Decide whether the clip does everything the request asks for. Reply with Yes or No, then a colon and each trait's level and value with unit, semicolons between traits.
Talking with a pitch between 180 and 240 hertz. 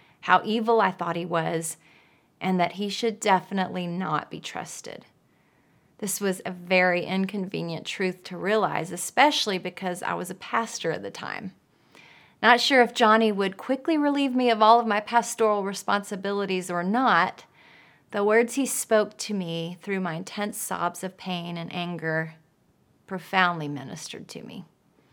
Yes: high, 190 Hz